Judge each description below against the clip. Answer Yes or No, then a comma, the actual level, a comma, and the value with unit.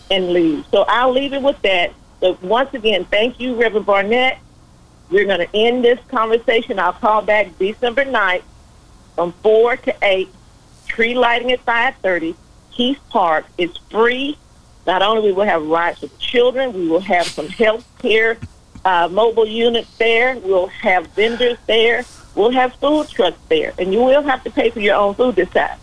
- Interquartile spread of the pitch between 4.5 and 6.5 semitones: Yes, average, 4.8 semitones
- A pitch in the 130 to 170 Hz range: No, high, 225 Hz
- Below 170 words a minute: No, average, 180 wpm